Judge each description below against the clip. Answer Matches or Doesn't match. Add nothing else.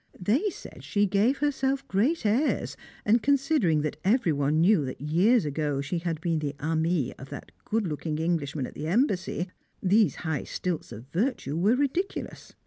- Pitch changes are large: Matches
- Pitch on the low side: Doesn't match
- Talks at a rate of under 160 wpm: Doesn't match